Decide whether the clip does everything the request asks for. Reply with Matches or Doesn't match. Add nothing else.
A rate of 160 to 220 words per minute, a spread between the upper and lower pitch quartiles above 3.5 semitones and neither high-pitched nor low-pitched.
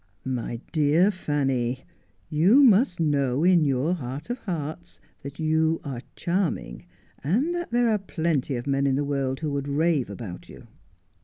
Matches